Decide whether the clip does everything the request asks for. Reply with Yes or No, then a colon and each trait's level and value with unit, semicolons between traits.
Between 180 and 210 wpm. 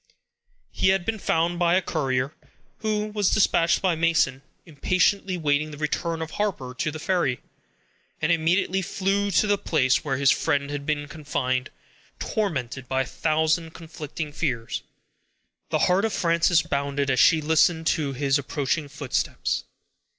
No: average, 150 wpm